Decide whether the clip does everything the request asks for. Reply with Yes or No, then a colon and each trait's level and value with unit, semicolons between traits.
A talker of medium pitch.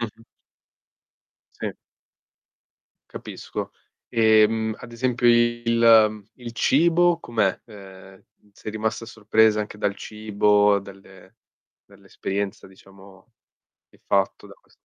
No: low, 110 Hz